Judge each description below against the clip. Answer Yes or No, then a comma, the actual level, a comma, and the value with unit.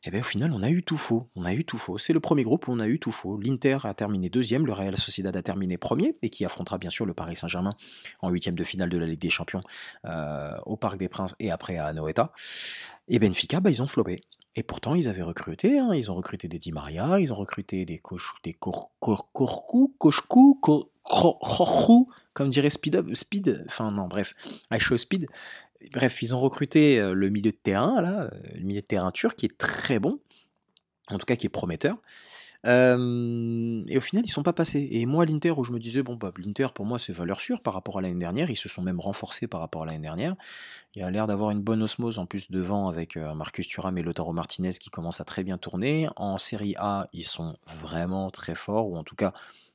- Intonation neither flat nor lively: No, wide, 6.5 semitones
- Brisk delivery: Yes, fast, 235 wpm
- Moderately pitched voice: No, low, 105 Hz